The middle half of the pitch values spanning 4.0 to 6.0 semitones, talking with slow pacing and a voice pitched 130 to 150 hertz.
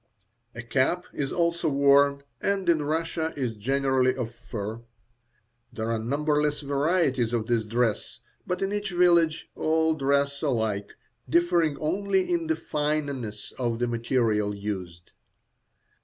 Yes: wide, 5.6 semitones; slow, 130 wpm; medium, 140 Hz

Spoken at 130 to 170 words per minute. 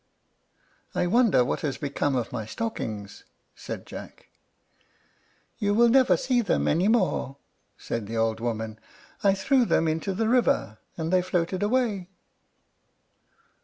Yes: slow, 135 wpm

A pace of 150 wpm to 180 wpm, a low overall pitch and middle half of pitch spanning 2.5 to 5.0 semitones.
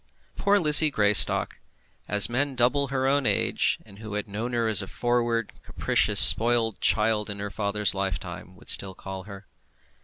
Yes: average, 165 wpm; low, 110 Hz; average, 3.4 semitones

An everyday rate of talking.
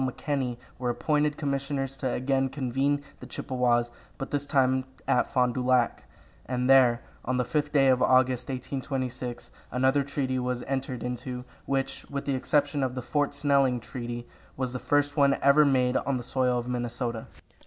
Yes: average, 170 wpm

